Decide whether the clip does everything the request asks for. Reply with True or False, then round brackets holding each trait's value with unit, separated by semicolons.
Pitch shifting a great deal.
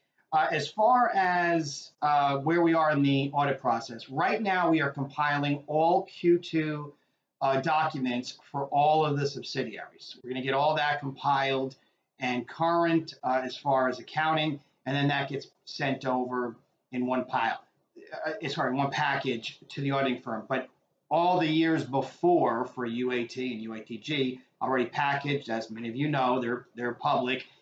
False (3.4 semitones)